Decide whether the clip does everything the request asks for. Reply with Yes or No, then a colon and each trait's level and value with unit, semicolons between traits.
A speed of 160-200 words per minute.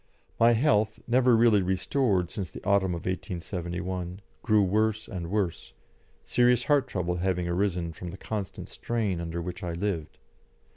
No: average, 150 wpm